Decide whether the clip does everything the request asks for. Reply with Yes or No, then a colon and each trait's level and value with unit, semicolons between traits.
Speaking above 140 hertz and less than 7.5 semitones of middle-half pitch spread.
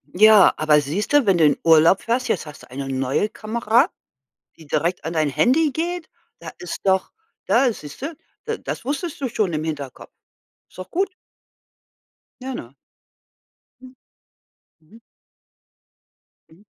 No: high, 190 Hz; wide, 8.8 semitones